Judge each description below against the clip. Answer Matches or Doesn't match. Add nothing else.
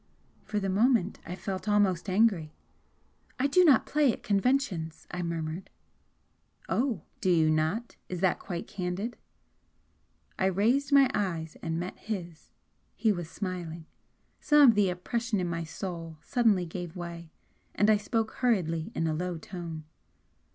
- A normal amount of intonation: Matches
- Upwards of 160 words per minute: Doesn't match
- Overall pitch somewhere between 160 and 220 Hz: Matches